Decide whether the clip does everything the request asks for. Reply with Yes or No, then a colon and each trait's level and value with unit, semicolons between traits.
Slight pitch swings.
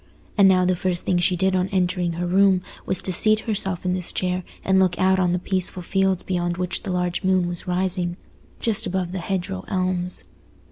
Yes: narrow, 1.1 semitones